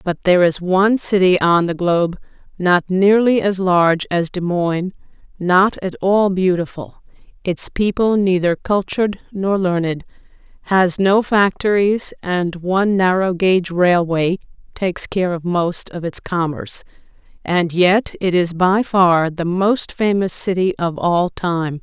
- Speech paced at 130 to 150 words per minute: Yes, average, 145 wpm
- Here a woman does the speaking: Yes, female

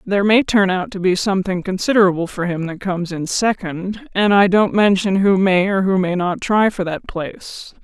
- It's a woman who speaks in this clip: Yes, female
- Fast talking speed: Yes, fast, 215 wpm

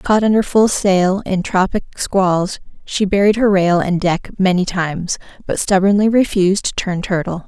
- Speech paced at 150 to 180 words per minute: Yes, average, 170 wpm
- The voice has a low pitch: No, high, 190 Hz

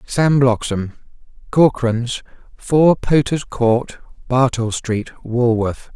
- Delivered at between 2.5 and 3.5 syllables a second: Yes, 3.1 syllables/s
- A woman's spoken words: No, male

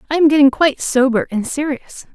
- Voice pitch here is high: Yes, very high, 280 Hz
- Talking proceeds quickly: No, average, 195 wpm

